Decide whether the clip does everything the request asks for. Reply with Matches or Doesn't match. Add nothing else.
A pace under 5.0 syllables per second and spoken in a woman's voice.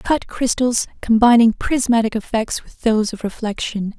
Matches